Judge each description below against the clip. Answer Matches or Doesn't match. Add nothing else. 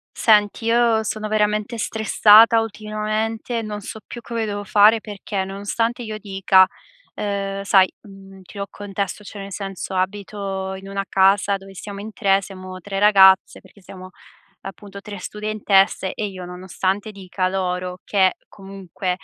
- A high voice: Matches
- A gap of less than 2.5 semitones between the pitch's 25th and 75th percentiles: Matches